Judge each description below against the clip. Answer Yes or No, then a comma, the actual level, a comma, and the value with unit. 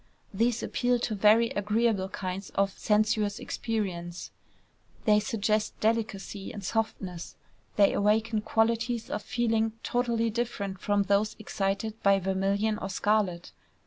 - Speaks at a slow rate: Yes, slow, 120 wpm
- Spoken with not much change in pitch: Yes, narrow, 2.3 semitones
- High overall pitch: Yes, high, 210 Hz